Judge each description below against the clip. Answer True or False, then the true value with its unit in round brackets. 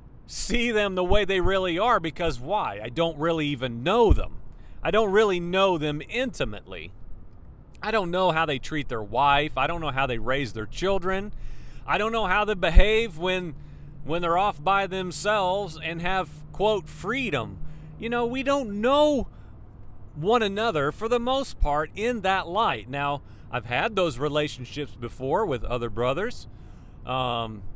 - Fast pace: False (165 wpm)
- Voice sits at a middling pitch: True (170 Hz)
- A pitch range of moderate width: False (7.6 semitones)